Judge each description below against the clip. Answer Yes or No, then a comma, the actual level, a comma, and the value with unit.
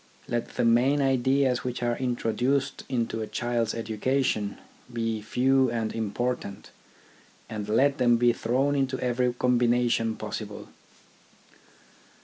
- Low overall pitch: Yes, low, 120 Hz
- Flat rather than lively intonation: Yes, narrow, 2.2 semitones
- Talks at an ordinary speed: No, slow, 125 wpm